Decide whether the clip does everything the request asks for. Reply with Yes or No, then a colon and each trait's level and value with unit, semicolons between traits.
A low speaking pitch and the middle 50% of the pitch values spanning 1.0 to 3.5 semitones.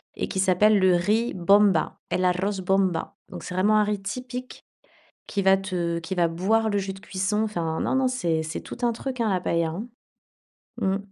No: high, 195 Hz; average, 3.0 semitones